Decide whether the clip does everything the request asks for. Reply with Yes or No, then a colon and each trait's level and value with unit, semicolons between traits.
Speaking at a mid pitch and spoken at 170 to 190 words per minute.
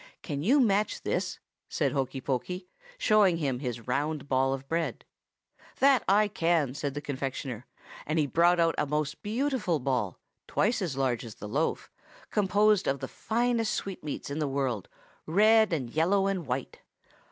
No: medium, 155 Hz; average, 160 wpm